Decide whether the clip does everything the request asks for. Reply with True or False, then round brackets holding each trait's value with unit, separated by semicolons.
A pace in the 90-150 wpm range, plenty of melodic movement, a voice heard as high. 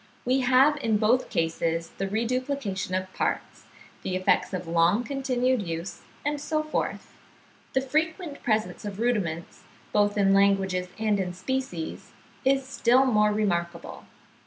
True (135 wpm; 5.9 semitones; 215 Hz)